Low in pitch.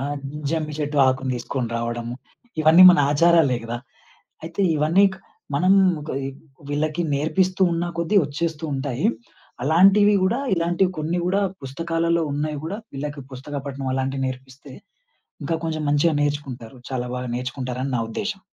No: medium, 150 Hz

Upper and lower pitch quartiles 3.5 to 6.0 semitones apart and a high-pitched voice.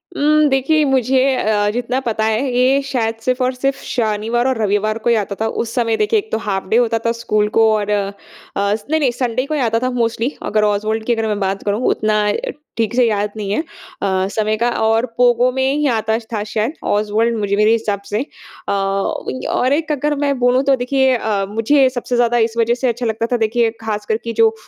No: average, 3.1 semitones; high, 230 Hz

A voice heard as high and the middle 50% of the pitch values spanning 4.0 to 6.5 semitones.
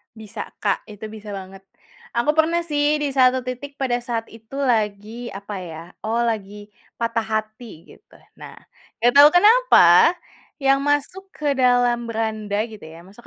Yes: high, 235 Hz; average, 4.7 semitones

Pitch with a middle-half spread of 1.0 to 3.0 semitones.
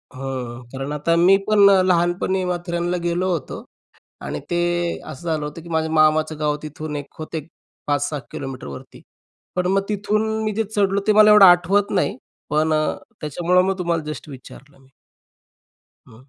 No: average, 3.8 semitones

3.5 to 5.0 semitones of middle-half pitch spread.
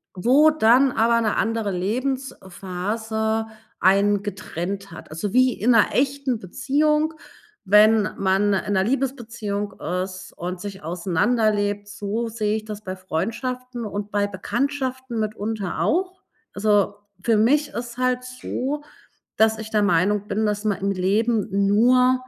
Yes: average, 3.9 semitones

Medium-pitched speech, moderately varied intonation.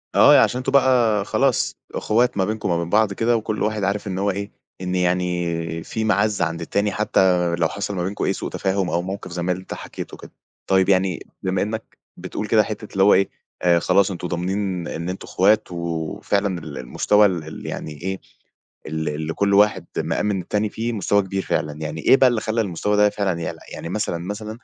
No: very low, 95 Hz; average, 3.2 semitones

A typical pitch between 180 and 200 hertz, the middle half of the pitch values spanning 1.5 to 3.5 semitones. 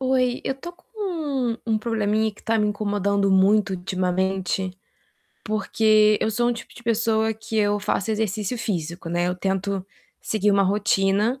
No: high, 210 Hz; average, 2.7 semitones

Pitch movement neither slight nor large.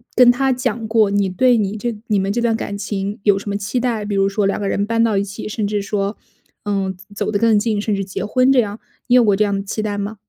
No: narrow, 2.3 semitones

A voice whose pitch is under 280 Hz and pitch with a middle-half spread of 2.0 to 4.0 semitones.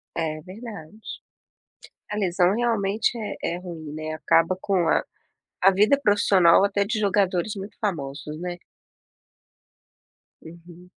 Yes: medium, 185 Hz; average, 3.6 semitones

